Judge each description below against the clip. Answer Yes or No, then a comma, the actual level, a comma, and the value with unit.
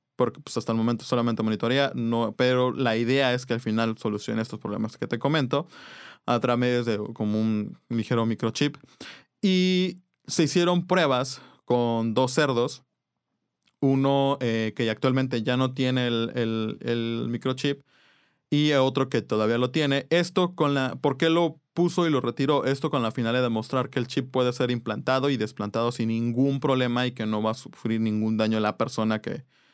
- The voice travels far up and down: No, average, 3.3 semitones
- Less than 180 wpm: No, average, 185 wpm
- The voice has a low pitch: Yes, low, 125 Hz